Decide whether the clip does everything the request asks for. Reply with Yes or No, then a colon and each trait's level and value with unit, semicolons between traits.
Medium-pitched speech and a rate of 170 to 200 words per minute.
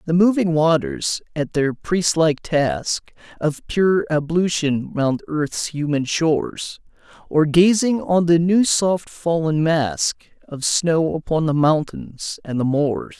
No: medium, 160 Hz; slow, 135 wpm